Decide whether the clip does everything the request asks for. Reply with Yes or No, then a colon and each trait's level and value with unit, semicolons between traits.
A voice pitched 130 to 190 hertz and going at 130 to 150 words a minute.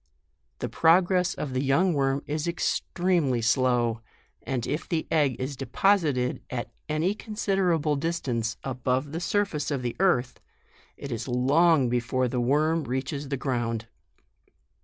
Yes: medium, 140 Hz; average, 140 wpm